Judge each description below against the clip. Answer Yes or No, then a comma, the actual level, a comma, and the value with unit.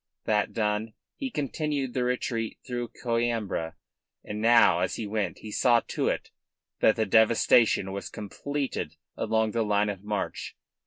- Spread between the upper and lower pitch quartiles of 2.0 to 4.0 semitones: Yes, narrow, 2.5 semitones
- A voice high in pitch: No, low, 110 Hz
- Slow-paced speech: No, average, 150 wpm